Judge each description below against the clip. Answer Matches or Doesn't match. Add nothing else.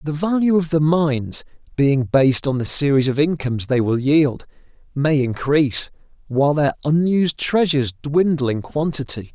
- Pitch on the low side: Doesn't match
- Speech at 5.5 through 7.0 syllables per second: Doesn't match